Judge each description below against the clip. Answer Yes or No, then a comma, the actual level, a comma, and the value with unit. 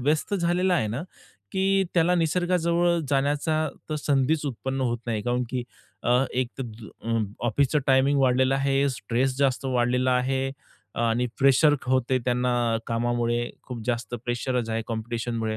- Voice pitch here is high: No, low, 130 Hz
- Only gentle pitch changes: No, average, 3.5 semitones